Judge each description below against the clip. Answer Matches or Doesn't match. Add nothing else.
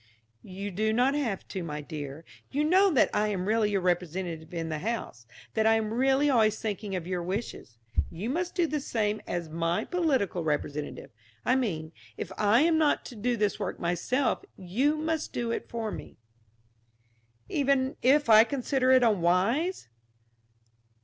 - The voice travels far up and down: Matches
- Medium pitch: Doesn't match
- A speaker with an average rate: Matches